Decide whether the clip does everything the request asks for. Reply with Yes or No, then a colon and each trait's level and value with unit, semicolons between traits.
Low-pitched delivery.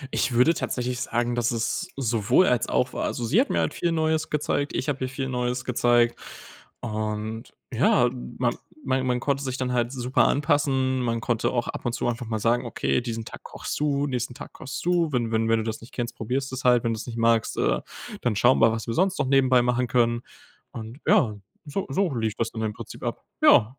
Yes: low, 125 Hz